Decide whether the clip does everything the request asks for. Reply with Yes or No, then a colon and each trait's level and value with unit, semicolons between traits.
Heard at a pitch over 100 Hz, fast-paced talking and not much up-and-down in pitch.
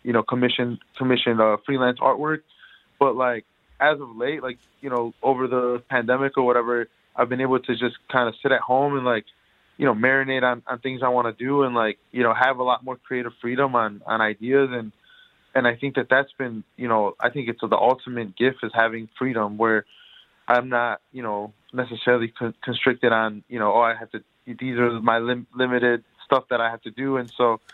Yes: low, 125 Hz; fast, 220 wpm; narrow, 1.9 semitones